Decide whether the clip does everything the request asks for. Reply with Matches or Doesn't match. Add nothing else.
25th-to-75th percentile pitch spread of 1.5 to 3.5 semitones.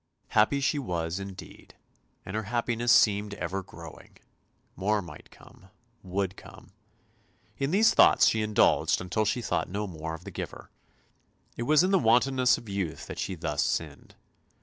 Doesn't match